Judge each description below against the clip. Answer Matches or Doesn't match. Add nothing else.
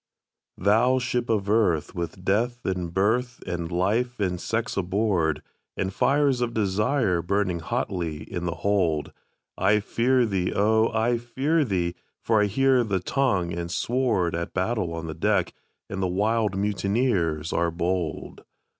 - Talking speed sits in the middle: Matches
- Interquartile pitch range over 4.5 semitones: Matches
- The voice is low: Matches